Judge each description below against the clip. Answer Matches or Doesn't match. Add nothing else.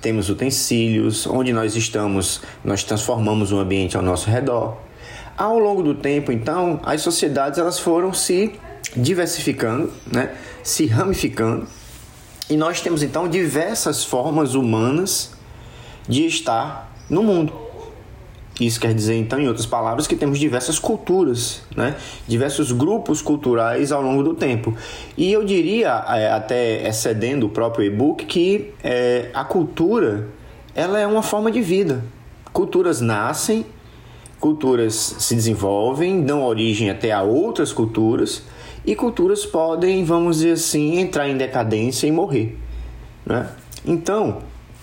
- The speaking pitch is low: Matches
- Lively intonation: Matches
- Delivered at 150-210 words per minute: Doesn't match